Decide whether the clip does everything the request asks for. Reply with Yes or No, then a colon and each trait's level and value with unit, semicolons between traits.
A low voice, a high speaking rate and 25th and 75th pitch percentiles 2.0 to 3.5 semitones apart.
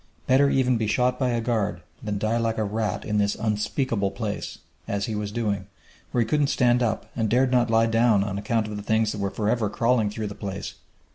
Yes: low, 110 Hz; fast, 225 wpm; narrow, 2.6 semitones